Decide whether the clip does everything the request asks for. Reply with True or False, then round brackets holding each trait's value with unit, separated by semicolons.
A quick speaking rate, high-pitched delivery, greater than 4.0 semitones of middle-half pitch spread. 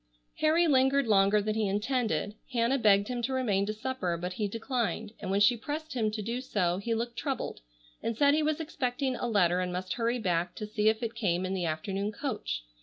True (220 wpm; 220 Hz; 4.4 semitones)